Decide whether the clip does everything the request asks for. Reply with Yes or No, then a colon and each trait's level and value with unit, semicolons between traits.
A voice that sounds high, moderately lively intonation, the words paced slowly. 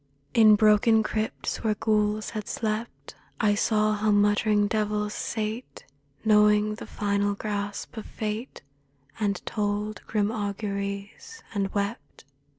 No: high, 210 Hz; narrow, 1.0 semitones; slow, 120 wpm